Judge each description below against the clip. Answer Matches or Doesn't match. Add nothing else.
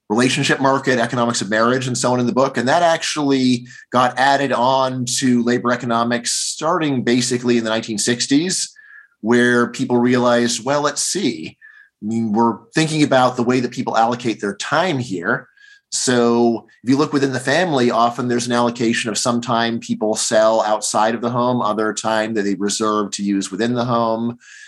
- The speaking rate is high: Doesn't match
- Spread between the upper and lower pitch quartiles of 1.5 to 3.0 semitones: Matches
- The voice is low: Matches